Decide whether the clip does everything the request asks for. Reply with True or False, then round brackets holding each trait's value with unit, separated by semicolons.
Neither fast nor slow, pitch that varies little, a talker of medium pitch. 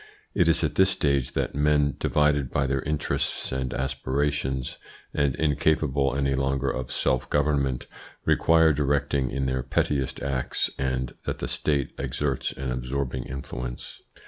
False (145 wpm; 1.8 semitones; 70 Hz)